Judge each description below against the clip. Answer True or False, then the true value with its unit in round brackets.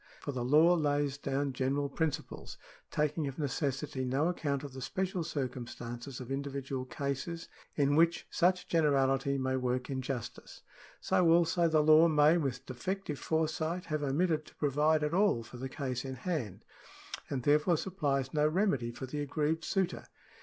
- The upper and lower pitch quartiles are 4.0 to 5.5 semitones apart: False (3.4 semitones)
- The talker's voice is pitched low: False (145 Hz)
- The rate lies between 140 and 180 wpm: True (160 wpm)